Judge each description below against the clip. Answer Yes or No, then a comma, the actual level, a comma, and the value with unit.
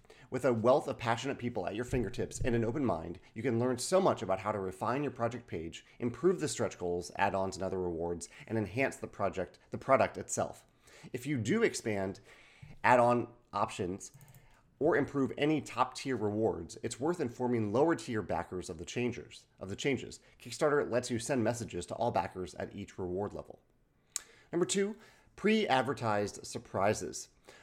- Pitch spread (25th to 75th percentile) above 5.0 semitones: Yes, wide, 5.4 semitones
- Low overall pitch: Yes, low, 115 Hz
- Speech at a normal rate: Yes, average, 165 wpm